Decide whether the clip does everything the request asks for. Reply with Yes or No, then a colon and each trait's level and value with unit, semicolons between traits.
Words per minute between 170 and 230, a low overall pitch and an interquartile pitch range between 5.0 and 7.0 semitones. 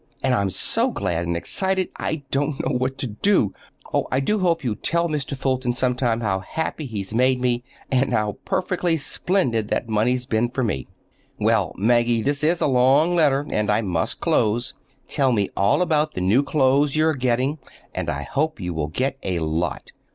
Yes: average, 195 wpm; low, 130 Hz; wide, 5.6 semitones